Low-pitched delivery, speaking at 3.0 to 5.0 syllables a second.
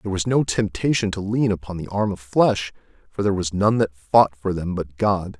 No: low, 100 Hz; 5.2 syllables/s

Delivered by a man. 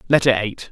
Yes: male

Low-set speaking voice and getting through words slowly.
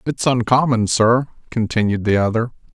Yes: low, 115 Hz; slow, 130 wpm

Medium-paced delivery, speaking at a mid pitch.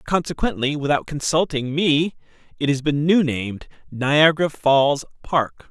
No: slow, 125 wpm; medium, 145 Hz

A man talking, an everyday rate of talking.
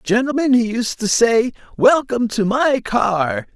Yes: male; average, 150 wpm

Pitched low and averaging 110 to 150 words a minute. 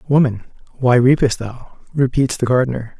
Yes: low, 125 Hz; average, 140 wpm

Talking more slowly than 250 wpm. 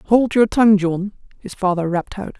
Yes: average, 200 wpm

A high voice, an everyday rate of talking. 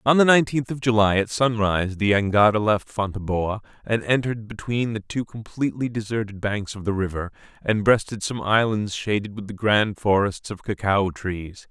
No: low, 105 Hz; average, 175 wpm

